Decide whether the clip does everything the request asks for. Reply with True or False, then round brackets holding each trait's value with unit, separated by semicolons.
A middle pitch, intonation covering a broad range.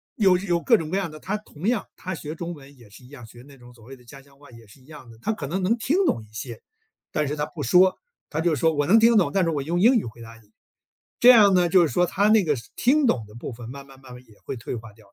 True (150 Hz; 7.0 semitones)